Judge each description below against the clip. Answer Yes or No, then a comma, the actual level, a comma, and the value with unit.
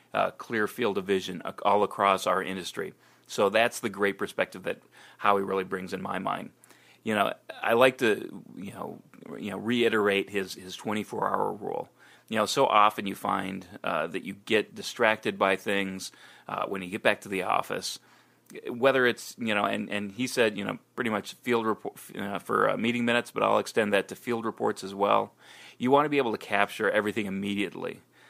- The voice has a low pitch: Yes, low, 100 Hz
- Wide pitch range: No, average, 2.9 semitones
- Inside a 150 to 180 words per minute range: No, fast, 205 wpm